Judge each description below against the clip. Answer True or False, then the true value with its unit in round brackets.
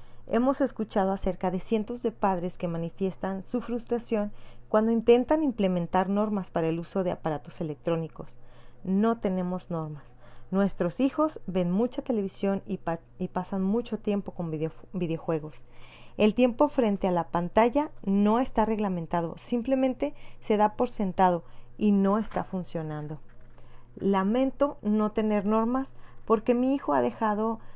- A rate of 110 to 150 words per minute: True (140 wpm)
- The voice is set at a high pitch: True (195 Hz)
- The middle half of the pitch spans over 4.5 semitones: True (5.0 semitones)